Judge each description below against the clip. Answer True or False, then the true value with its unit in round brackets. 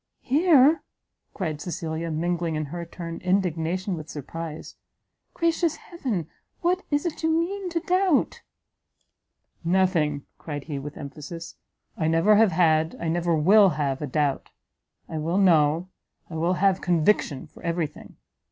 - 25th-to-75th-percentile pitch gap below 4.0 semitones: False (4.8 semitones)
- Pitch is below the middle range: False (170 Hz)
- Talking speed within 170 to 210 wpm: False (145 wpm)